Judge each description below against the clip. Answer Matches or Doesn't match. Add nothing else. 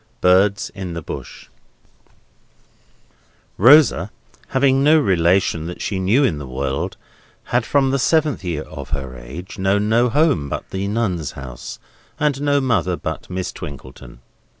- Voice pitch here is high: Doesn't match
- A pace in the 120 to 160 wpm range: Matches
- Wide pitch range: Matches